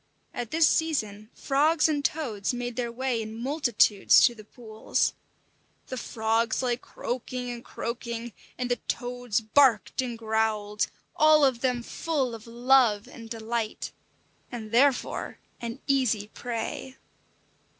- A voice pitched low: No, high, 240 Hz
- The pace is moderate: No, slow, 130 wpm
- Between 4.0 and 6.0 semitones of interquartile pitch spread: No, average, 2.7 semitones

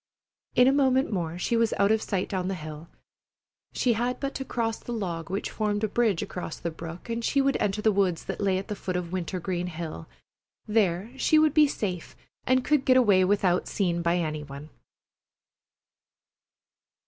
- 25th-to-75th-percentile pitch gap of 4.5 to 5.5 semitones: Yes, average, 5.2 semitones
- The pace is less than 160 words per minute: No, average, 190 wpm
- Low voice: No, high, 195 Hz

